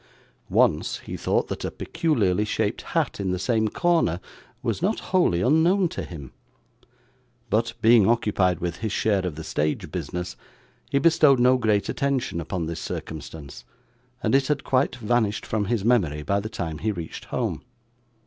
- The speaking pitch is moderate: No, low, 105 Hz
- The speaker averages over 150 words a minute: Yes, average, 165 wpm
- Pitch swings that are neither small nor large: No, wide, 6.5 semitones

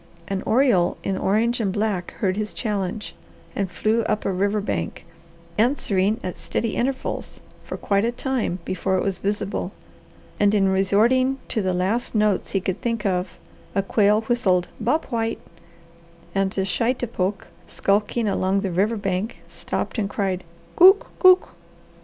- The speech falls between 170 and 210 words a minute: No, average, 155 wpm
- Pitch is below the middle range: No, high, 205 Hz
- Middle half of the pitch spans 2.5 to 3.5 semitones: Yes, average, 3.2 semitones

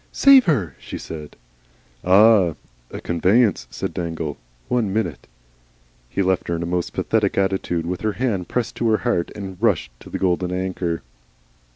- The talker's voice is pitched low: Yes, very low, 95 Hz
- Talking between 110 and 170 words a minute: Yes, average, 165 wpm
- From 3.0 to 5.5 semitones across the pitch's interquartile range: Yes, average, 4.1 semitones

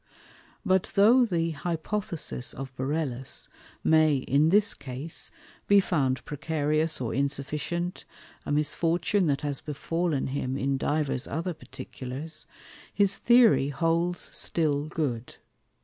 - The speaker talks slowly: Yes, slow, 115 wpm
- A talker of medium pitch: Yes, medium, 155 Hz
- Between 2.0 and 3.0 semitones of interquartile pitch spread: No, average, 3.8 semitones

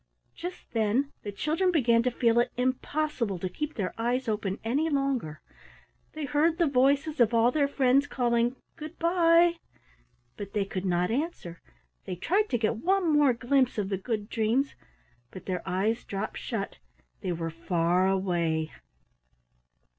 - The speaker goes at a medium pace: Yes, average, 155 wpm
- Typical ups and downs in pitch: No, wide, 6.7 semitones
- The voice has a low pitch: No, high, 240 Hz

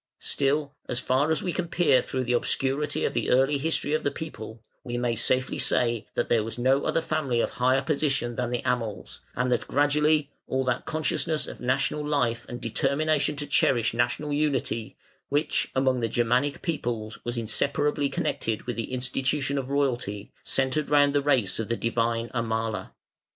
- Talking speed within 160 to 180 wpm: Yes, average, 175 wpm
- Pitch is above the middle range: No, low, 130 Hz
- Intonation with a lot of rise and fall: No, average, 3.5 semitones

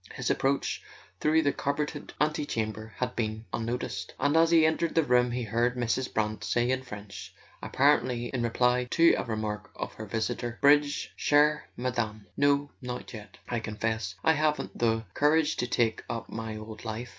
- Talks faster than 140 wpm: Yes, average, 170 wpm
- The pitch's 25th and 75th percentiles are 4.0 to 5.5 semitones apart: Yes, average, 4.4 semitones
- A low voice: Yes, low, 125 Hz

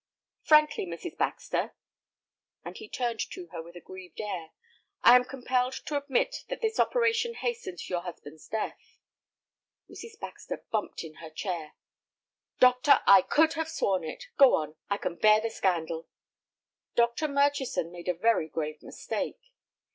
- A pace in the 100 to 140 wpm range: No, average, 150 wpm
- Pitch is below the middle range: No, high, 230 Hz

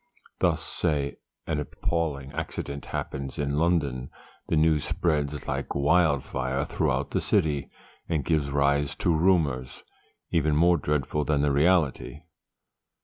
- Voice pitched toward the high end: No, very low, 75 Hz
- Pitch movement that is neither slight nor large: No, narrow, 2.2 semitones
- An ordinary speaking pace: No, slow, 125 wpm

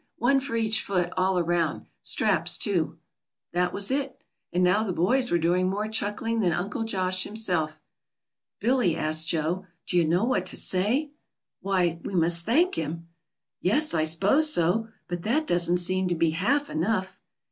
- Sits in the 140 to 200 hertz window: Yes, medium, 185 Hz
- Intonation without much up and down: No, average, 4.5 semitones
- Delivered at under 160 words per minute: No, average, 170 wpm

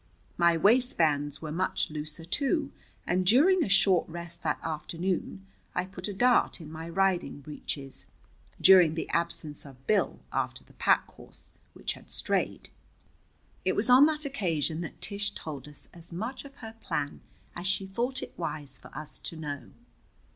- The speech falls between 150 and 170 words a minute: Yes, average, 165 wpm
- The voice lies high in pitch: No, medium, 175 Hz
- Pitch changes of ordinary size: Yes, average, 4.8 semitones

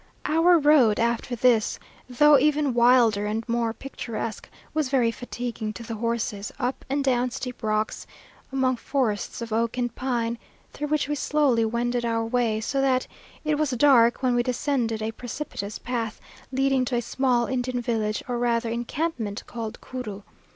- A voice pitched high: Yes, high, 240 Hz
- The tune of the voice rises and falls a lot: No, narrow, 2.6 semitones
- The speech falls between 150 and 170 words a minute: Yes, average, 165 wpm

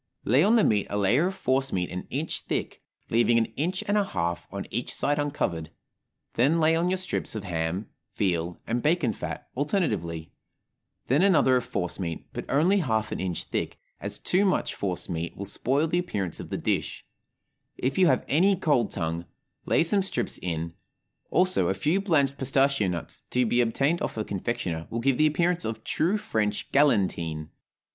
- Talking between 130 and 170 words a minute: No, average, 185 wpm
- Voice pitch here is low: Yes, low, 125 Hz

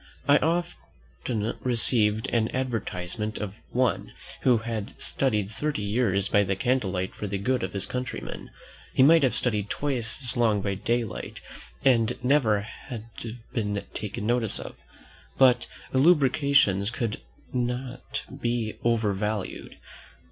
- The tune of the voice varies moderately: Yes, average, 3.7 semitones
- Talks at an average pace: No, slow, 125 wpm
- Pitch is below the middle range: Yes, low, 115 Hz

